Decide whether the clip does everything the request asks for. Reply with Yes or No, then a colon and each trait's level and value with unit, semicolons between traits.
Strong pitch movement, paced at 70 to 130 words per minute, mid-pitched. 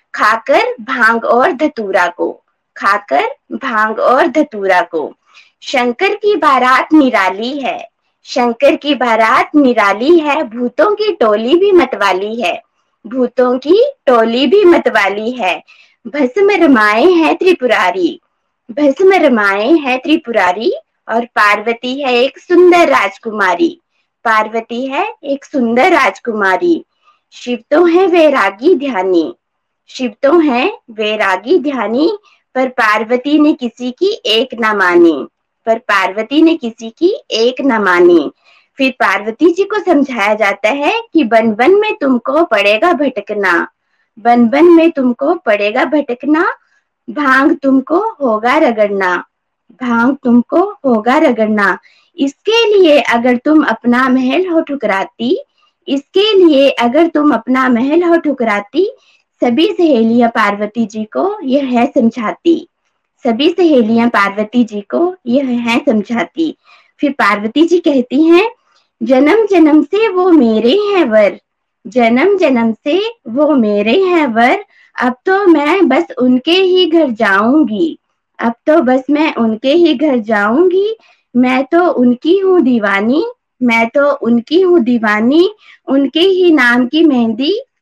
No: wide, 6.4 semitones; average, 125 wpm; very high, 275 Hz